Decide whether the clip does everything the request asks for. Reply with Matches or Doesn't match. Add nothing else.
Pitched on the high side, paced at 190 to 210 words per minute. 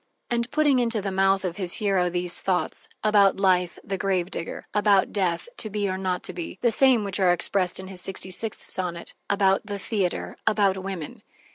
Matches